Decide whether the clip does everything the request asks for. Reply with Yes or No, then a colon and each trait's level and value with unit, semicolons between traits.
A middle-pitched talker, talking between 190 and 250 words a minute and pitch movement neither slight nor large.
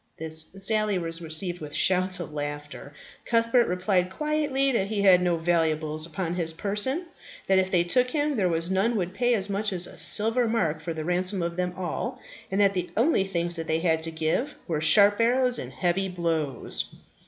Yes: medium, 180 Hz; average, 200 wpm; average, 4.4 semitones